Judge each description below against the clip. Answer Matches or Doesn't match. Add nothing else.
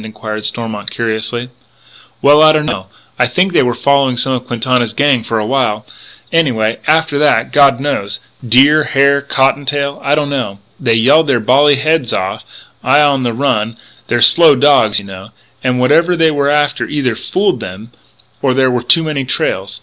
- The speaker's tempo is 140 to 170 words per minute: Doesn't match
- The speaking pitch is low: Matches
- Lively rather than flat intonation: Doesn't match